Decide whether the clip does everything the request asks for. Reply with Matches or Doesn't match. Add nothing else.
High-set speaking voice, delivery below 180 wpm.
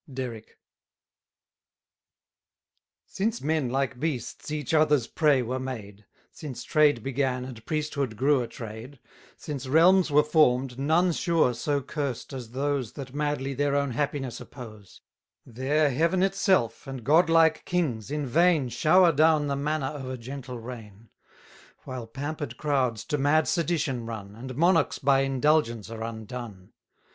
Doesn't match